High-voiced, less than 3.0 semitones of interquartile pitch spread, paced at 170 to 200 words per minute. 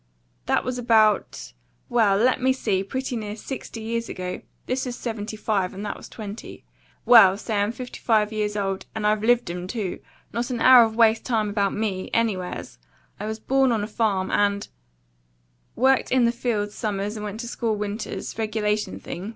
Yes: high, 215 Hz; narrow, 2.6 semitones; average, 185 wpm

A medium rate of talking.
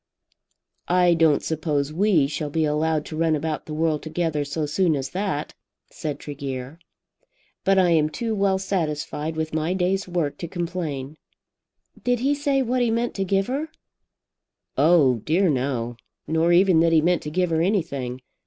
Yes: average, 170 wpm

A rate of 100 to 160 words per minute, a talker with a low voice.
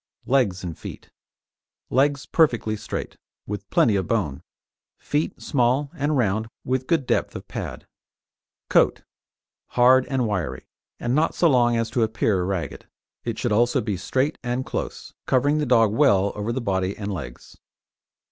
Yes: average, 155 wpm; low, 120 Hz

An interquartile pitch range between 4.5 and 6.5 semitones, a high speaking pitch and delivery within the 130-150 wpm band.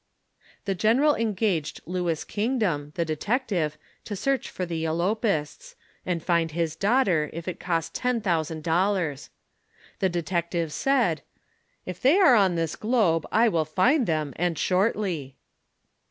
No: average, 5.1 semitones; medium, 180 Hz; average, 140 wpm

